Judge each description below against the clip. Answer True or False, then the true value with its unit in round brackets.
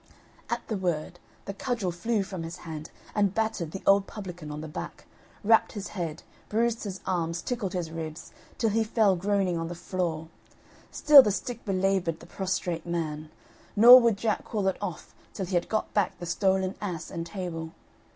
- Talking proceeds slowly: False (185 wpm)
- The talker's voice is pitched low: False (185 Hz)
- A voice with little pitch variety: False (3.8 semitones)